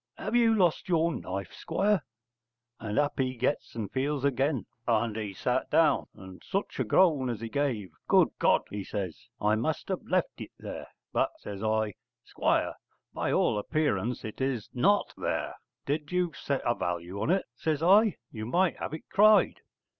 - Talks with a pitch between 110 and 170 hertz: Yes, low, 135 Hz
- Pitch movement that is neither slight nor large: No, wide, 7.6 semitones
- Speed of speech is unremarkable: Yes, average, 175 wpm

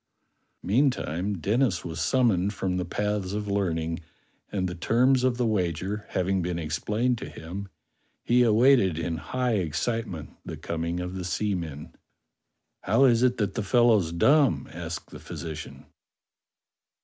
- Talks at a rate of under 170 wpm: Yes, average, 150 wpm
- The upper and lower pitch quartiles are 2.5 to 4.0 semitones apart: No, average, 5.3 semitones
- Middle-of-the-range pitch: No, very low, 95 Hz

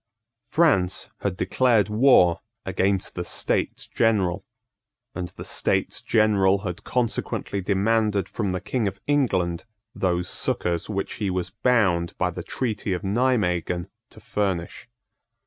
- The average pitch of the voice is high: No, low, 100 Hz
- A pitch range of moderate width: Yes, average, 3.7 semitones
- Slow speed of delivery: Yes, slow, 130 wpm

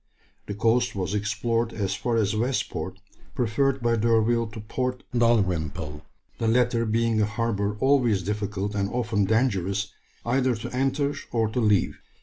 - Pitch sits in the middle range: No, low, 115 Hz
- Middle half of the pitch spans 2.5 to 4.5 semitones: Yes, average, 2.8 semitones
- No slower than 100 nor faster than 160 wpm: Yes, average, 150 wpm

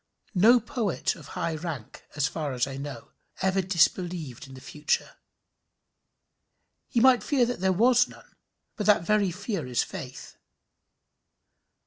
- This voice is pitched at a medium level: Yes, medium, 180 Hz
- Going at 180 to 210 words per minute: No, average, 140 wpm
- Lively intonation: Yes, wide, 6.5 semitones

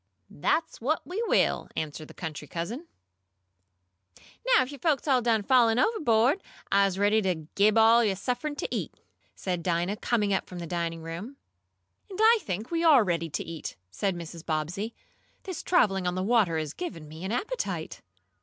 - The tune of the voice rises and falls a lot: Yes, wide, 6.9 semitones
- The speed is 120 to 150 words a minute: No, average, 180 wpm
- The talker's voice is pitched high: Yes, high, 205 Hz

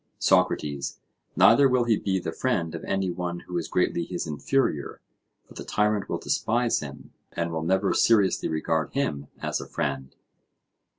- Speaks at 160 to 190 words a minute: Yes, average, 165 wpm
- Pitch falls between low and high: No, very low, 90 Hz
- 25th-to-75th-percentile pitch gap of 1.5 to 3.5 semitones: No, average, 5.0 semitones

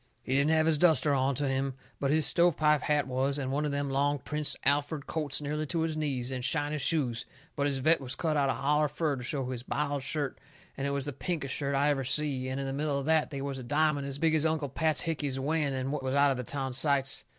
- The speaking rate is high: Yes, fast, 255 wpm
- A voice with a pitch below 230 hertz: Yes, medium, 140 Hz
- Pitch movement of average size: No, narrow, 2.1 semitones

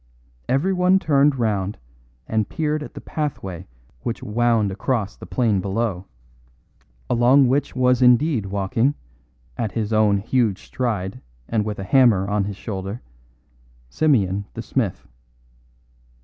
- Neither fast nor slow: No, slow, 125 wpm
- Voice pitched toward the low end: Yes, low, 115 Hz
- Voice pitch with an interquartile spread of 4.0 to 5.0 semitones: Yes, average, 4.6 semitones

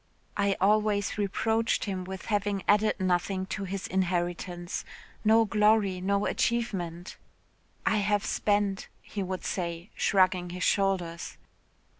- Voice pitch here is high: Yes, high, 195 Hz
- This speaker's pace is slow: Yes, slow, 120 wpm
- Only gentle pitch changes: Yes, narrow, 2.2 semitones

